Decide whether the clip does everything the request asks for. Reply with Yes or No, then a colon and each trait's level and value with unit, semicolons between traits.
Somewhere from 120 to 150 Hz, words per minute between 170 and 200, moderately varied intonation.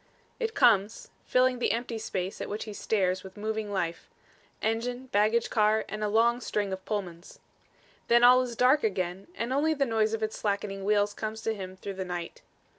No: high, 215 Hz; average, 190 wpm; average, 3.1 semitones